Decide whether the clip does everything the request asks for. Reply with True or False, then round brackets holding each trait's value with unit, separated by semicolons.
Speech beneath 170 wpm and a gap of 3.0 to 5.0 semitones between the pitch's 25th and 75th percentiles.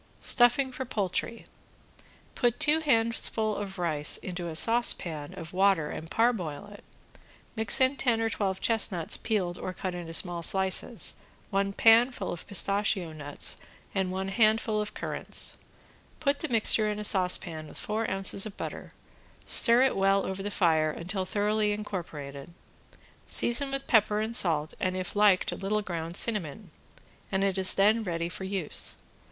True (160 wpm; 3.9 semitones)